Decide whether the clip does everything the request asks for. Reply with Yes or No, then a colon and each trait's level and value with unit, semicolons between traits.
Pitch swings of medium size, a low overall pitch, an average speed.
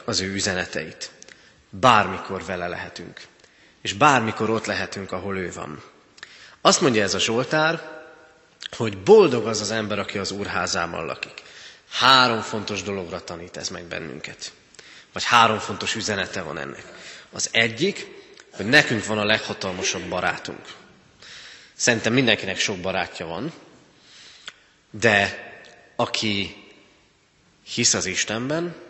Yes: average, 3.9 semitones; low, 105 Hz; average, 120 wpm